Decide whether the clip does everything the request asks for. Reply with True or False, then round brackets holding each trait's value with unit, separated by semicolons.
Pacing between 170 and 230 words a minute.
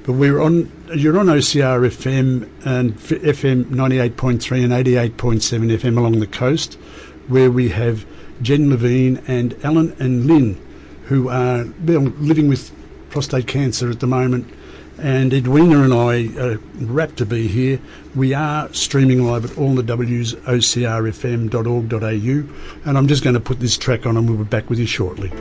True (175 wpm)